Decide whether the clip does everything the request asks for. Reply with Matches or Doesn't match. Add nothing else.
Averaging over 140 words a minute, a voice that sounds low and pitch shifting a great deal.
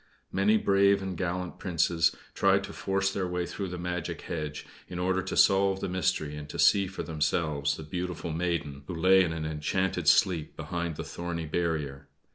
Doesn't match